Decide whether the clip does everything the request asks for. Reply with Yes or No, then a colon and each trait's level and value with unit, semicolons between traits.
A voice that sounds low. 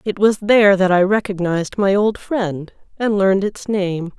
No: high, 195 Hz